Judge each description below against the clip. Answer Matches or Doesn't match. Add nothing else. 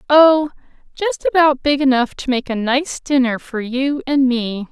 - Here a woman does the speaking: Matches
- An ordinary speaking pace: Matches